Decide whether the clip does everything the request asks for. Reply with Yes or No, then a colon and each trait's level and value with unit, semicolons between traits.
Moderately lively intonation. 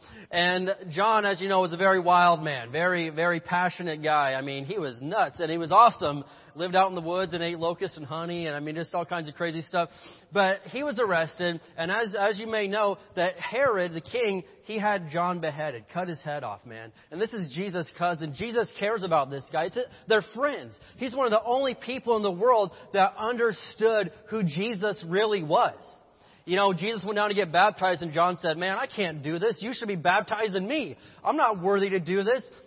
Yes: average, 4.2 semitones